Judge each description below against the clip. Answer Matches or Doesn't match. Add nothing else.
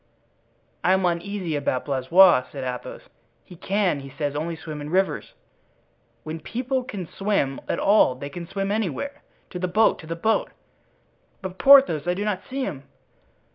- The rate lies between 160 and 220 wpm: Matches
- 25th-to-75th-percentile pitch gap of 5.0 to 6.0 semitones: Matches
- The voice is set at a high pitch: Doesn't match